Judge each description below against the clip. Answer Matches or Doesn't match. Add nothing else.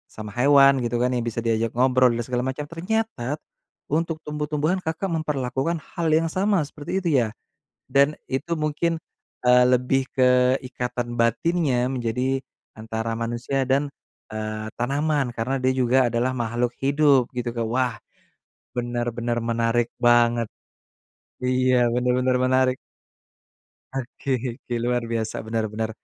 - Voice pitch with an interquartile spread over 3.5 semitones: Doesn't match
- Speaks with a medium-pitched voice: Doesn't match